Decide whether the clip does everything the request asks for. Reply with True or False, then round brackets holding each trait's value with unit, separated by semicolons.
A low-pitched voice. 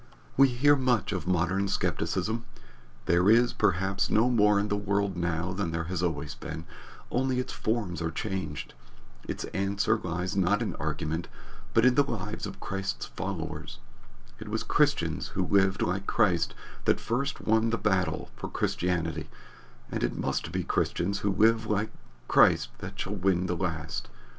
True (95 Hz)